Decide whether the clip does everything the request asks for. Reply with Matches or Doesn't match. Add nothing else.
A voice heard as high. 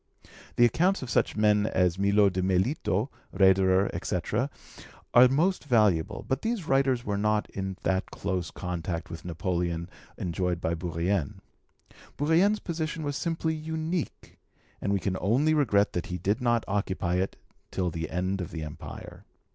Doesn't match